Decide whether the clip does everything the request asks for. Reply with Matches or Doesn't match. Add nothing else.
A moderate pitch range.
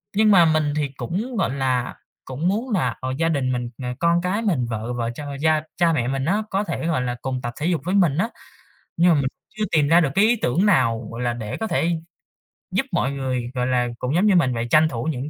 Doesn't match